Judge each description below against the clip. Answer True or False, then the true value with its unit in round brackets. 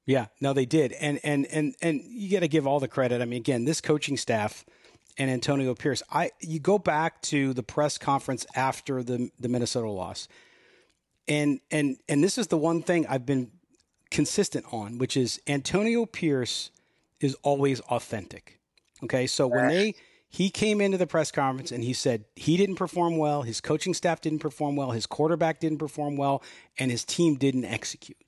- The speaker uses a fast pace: False (185 wpm)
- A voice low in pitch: False (145 Hz)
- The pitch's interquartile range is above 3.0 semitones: True (3.8 semitones)